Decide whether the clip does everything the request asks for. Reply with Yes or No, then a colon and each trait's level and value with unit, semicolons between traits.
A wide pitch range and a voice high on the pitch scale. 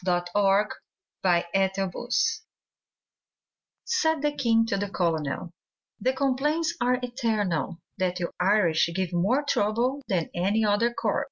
Yes: wide, 5.7 semitones; high, 205 Hz